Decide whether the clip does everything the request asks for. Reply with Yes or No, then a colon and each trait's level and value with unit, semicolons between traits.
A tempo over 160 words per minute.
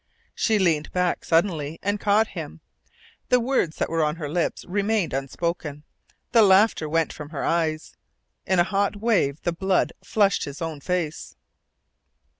No: average, 155 wpm